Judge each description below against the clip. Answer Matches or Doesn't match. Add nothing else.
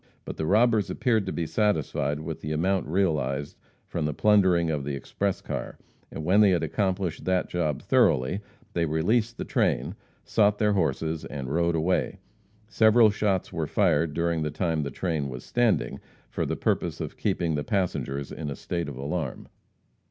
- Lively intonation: Doesn't match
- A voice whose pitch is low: Matches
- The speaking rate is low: Doesn't match